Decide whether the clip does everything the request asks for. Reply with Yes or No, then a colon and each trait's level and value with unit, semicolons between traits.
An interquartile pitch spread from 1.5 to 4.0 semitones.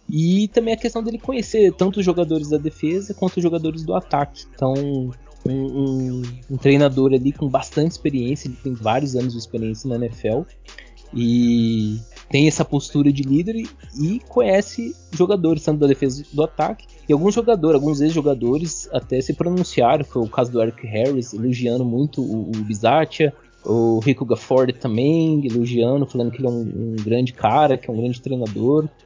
No: average, 4.8 semitones